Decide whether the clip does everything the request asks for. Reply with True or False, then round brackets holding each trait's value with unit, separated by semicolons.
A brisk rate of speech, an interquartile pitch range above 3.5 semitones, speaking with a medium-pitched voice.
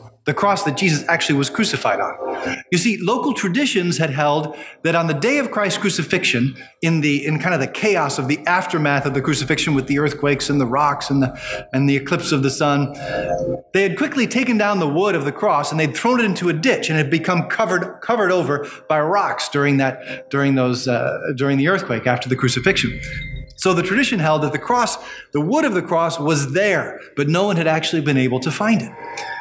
True (220 wpm; 5.4 semitones; 155 Hz)